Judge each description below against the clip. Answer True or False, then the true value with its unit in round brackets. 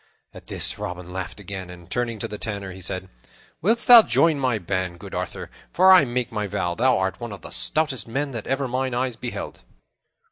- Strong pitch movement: True (5.7 semitones)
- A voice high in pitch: False (115 Hz)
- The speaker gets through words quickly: True (210 wpm)